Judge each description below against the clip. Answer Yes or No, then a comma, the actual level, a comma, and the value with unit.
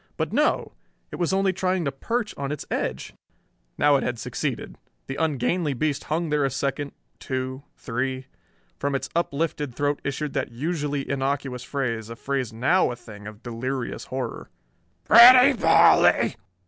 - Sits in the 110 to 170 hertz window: Yes, medium, 140 Hz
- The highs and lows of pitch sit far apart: No, average, 3.4 semitones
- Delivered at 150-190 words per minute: Yes, average, 155 wpm